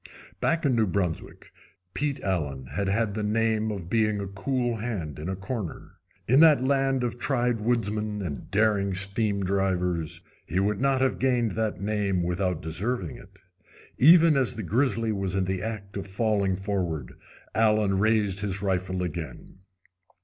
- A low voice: Yes, low, 100 Hz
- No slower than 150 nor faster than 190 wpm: Yes, average, 160 wpm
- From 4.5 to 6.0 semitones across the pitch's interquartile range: No, average, 3.4 semitones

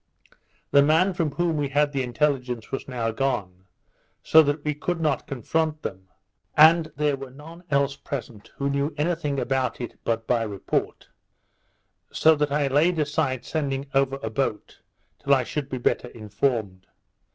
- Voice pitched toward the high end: No, medium, 140 Hz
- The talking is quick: No, average, 165 wpm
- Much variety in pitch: No, average, 3.3 semitones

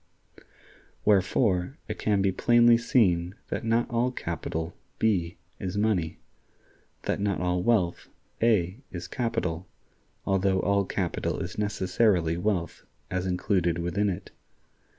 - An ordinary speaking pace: No, slow, 120 wpm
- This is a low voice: Yes, very low, 95 Hz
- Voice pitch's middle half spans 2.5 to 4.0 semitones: Yes, average, 3.6 semitones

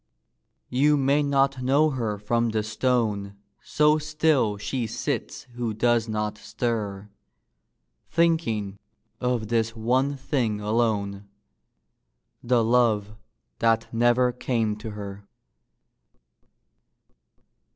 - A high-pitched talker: No, low, 115 Hz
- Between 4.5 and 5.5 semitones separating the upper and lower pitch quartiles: No, average, 3.4 semitones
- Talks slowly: Yes, slow, 100 wpm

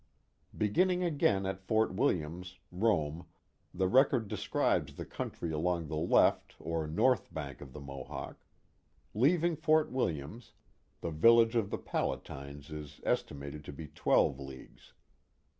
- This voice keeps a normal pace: No, slow, 130 wpm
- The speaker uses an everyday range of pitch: No, wide, 7.6 semitones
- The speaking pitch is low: Yes, very low, 90 Hz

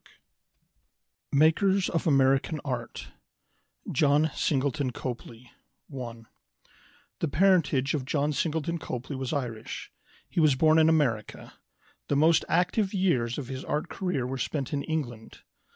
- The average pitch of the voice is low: No, medium, 145 Hz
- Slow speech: Yes, slow, 130 wpm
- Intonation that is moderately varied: Yes, average, 3.8 semitones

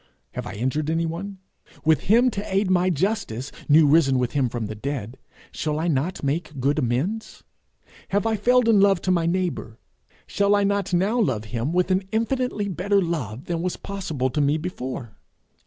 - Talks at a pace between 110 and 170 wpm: No, average, 185 wpm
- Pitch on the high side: No, medium, 170 Hz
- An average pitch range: No, wide, 6.4 semitones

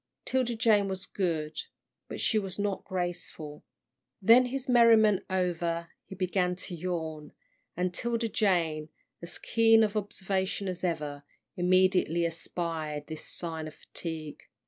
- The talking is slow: Yes, slow, 130 wpm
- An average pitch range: Yes, average, 3.8 semitones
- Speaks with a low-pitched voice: No, medium, 180 Hz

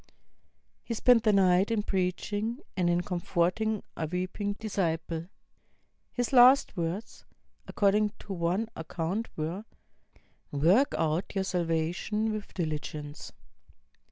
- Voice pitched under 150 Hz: No, medium, 185 Hz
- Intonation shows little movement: No, average, 4.2 semitones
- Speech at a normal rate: No, slow, 110 wpm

